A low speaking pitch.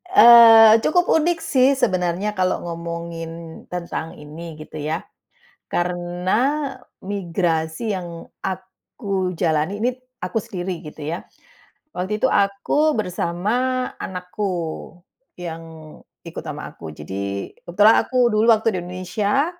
No: medium, 180 Hz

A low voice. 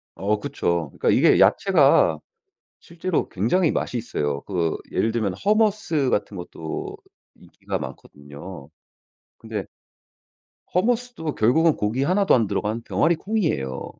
Yes: low, 115 Hz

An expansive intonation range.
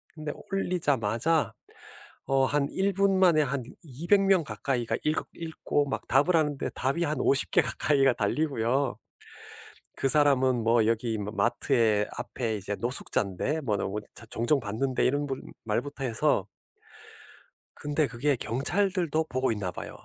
No: average, 4.8 semitones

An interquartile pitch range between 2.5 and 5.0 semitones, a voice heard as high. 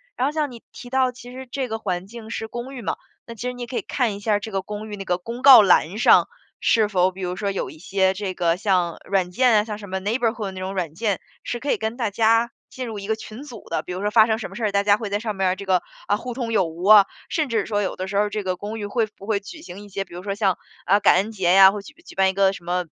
Yes: average, 3.2 semitones; high, 205 Hz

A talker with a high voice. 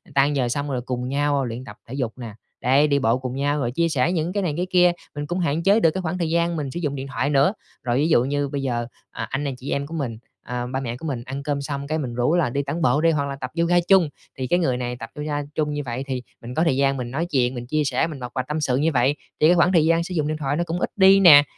No: medium, 140 Hz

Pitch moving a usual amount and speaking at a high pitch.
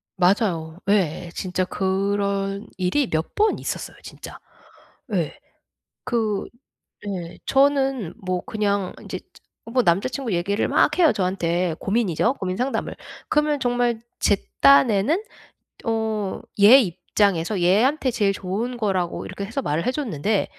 Yes: average, 4.9 semitones; high, 200 Hz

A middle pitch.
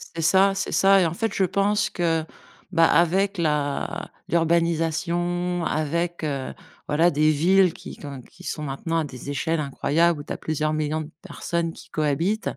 Yes: medium, 165 Hz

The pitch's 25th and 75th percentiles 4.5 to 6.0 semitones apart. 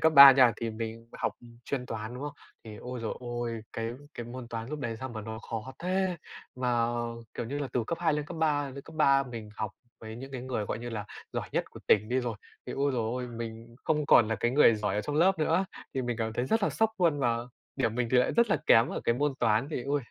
No: average, 4.1 semitones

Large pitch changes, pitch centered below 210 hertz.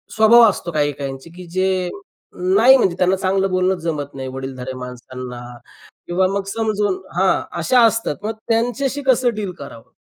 Yes: wide, 7.2 semitones; medium, 185 Hz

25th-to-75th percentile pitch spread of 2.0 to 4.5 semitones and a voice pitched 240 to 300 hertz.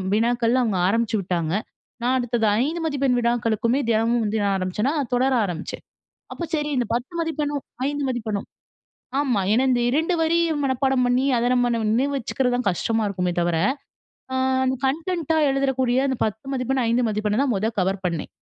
Yes: average, 3.8 semitones; high, 245 Hz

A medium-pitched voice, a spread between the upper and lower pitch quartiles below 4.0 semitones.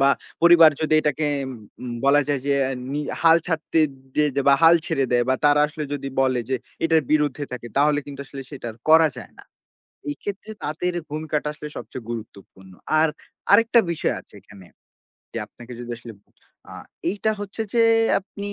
Yes: medium, 150 Hz; average, 3.6 semitones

